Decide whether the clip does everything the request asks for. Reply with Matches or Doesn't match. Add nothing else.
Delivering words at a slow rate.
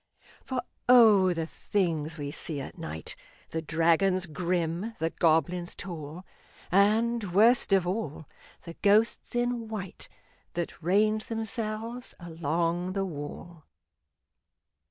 Matches